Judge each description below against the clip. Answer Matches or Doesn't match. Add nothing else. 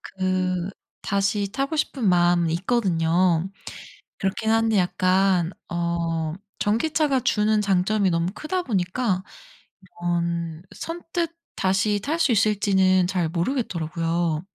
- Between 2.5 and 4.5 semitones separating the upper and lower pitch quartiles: Matches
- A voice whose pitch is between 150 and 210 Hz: Matches